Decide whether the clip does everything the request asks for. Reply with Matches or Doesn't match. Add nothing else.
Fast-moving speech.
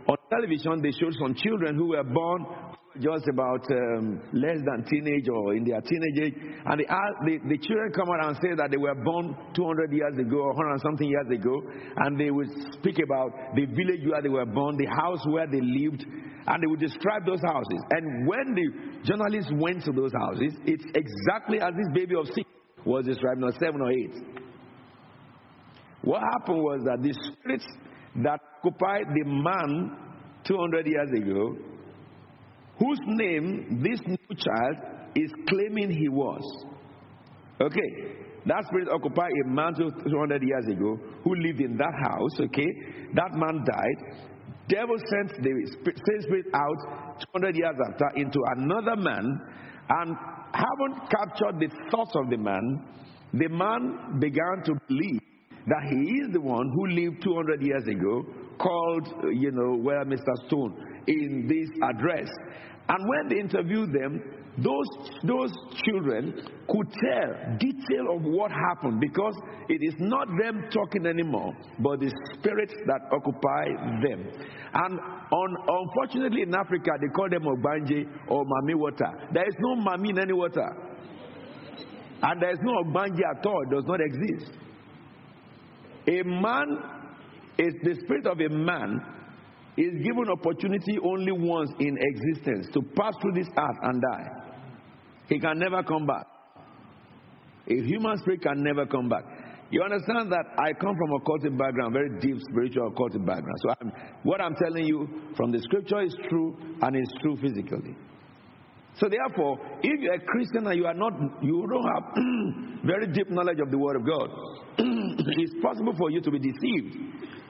Doesn't match